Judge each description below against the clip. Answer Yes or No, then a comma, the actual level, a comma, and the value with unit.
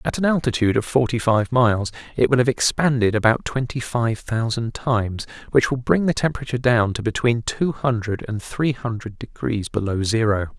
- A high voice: No, low, 120 Hz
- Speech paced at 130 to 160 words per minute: No, average, 180 wpm